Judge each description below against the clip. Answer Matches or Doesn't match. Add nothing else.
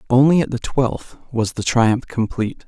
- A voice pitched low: Matches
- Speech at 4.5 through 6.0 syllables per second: Matches